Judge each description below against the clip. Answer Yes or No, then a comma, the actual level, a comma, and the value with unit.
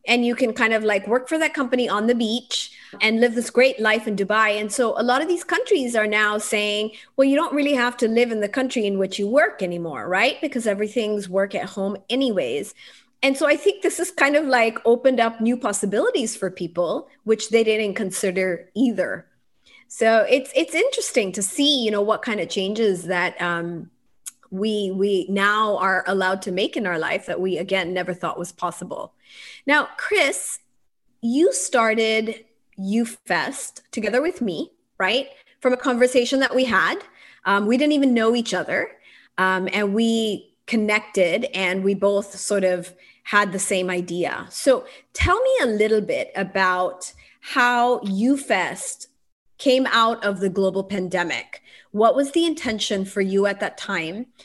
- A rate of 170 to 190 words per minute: Yes, average, 180 wpm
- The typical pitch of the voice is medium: No, high, 220 Hz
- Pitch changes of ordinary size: Yes, average, 4.7 semitones